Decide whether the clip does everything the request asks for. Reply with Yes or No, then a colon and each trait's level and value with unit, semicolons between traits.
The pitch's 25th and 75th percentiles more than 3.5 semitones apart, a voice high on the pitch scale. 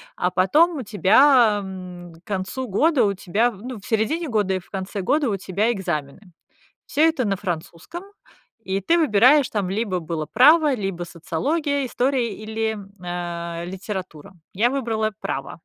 Yes: wide, 5.6 semitones; high, 205 Hz